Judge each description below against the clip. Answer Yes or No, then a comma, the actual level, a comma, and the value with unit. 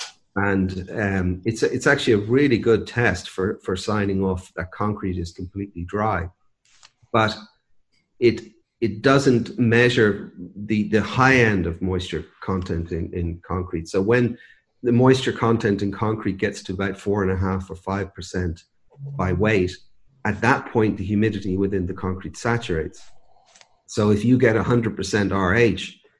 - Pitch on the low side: Yes, low, 100 Hz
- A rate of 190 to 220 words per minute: No, average, 160 wpm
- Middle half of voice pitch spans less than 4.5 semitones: Yes, average, 3.4 semitones